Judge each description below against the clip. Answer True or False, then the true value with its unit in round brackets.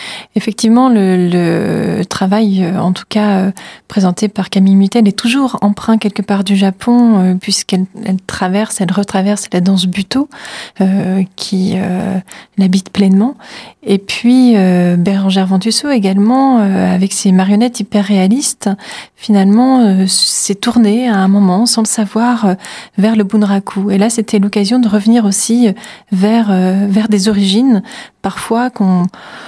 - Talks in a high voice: True (205 Hz)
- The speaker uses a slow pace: True (140 wpm)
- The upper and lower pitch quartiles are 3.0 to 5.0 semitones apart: False (2.6 semitones)